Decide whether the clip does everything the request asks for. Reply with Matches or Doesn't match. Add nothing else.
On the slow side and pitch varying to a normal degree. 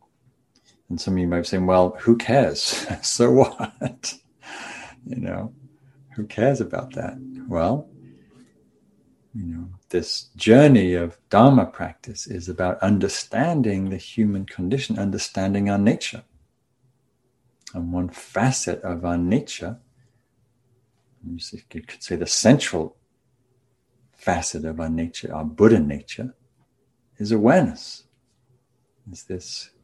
Doesn't match